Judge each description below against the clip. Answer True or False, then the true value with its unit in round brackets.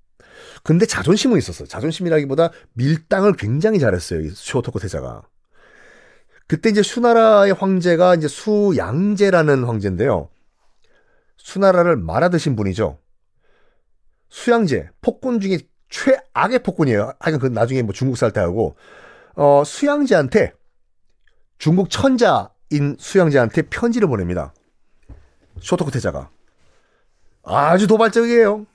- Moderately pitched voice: True (175 Hz)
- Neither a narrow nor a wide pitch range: False (7.1 semitones)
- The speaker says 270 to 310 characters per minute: True (280 characters per minute)